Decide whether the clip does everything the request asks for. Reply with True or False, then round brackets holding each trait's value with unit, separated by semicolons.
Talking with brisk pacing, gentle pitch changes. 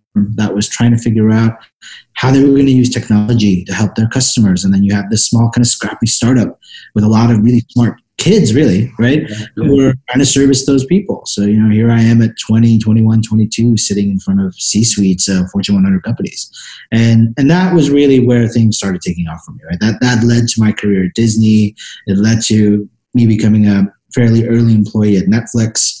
True (220 wpm; 2.3 semitones)